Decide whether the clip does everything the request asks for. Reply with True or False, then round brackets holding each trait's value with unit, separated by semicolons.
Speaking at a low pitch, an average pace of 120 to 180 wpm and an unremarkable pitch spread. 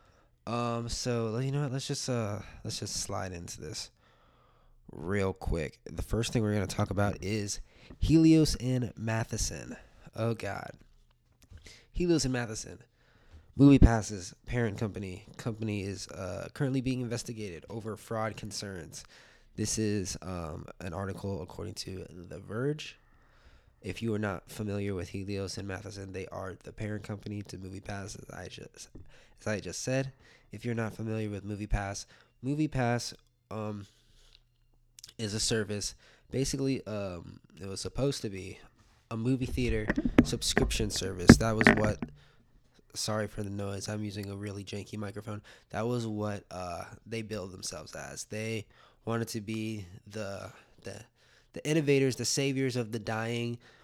True (110 Hz; 150 wpm; 3.3 semitones)